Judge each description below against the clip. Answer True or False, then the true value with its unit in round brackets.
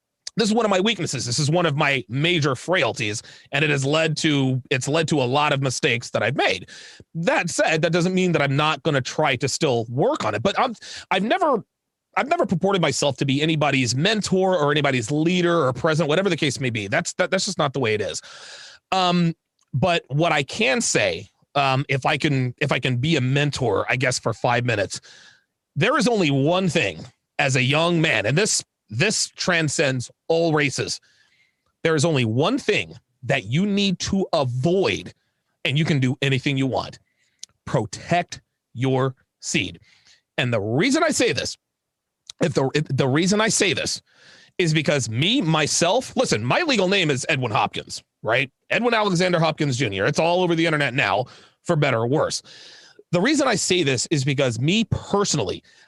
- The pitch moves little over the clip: False (4.3 semitones)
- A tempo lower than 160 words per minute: False (190 wpm)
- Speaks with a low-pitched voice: False (155 Hz)